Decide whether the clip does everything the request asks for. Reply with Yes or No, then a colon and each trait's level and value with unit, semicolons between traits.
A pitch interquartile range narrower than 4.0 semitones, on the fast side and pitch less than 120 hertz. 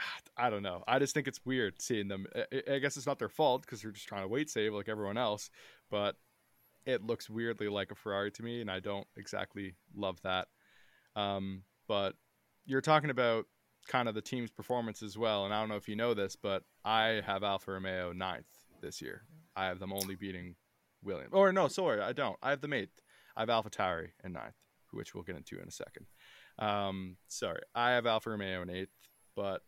Yes: average, 3.5 semitones; fast, 215 wpm; low, 105 Hz